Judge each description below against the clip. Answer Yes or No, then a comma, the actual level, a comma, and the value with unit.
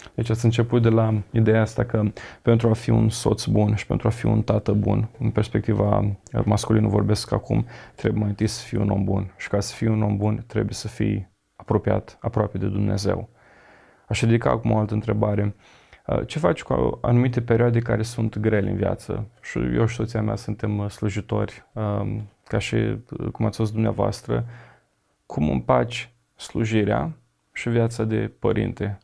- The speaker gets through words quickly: Yes, fast, 175 wpm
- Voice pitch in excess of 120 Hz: No, low, 110 Hz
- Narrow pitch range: Yes, narrow, 1.8 semitones